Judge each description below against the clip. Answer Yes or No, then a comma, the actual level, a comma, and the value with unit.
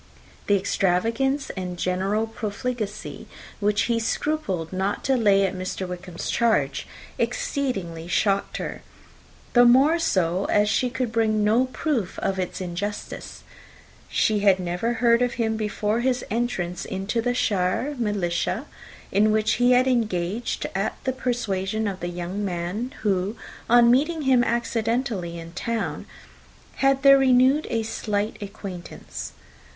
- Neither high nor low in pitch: No, high, 215 Hz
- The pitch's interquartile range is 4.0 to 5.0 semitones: Yes, average, 4.4 semitones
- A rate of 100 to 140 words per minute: Yes, slow, 135 wpm